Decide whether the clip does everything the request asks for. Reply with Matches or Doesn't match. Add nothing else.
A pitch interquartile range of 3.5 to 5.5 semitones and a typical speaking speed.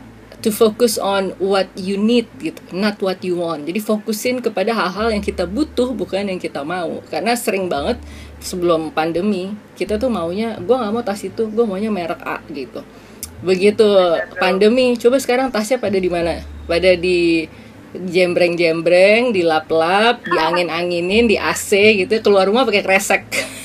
Matches